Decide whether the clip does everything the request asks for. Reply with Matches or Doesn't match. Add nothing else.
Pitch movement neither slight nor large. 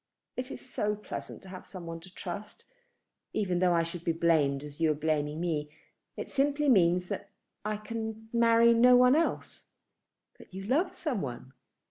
Doesn't match